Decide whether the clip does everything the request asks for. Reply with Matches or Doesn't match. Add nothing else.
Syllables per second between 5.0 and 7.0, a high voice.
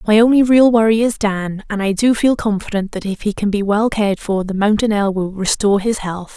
Matches